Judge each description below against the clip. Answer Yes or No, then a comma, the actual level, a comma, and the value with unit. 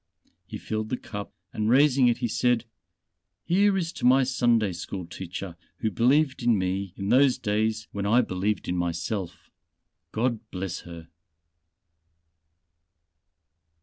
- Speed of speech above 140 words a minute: No, slow, 135 wpm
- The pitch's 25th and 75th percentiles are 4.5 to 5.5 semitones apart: Yes, average, 4.8 semitones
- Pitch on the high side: No, low, 110 Hz